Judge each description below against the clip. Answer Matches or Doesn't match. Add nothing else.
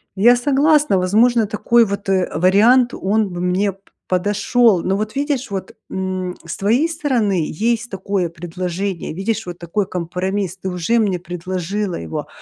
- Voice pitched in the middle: Doesn't match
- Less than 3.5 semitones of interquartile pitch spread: Doesn't match